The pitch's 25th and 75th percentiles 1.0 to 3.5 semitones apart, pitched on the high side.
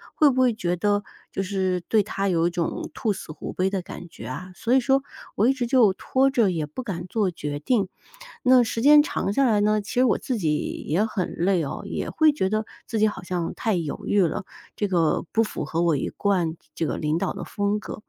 No: average, 4.7 semitones; high, 200 Hz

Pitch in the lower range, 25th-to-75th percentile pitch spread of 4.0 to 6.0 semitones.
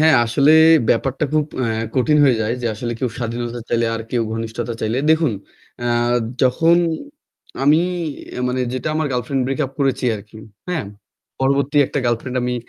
No: low, 125 Hz; average, 2.9 semitones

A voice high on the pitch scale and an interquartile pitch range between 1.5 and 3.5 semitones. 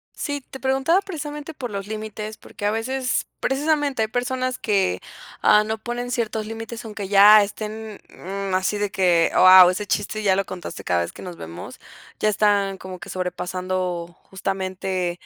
No: high, 210 Hz; average, 4.3 semitones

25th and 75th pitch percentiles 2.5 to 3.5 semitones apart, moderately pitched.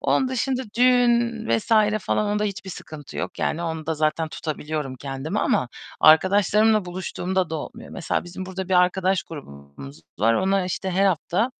No: average, 4.9 semitones; medium, 180 Hz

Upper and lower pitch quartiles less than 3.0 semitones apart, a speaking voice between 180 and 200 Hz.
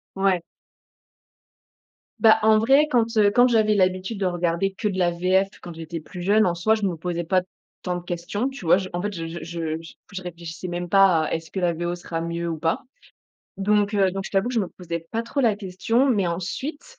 No: average, 3.5 semitones; medium, 185 Hz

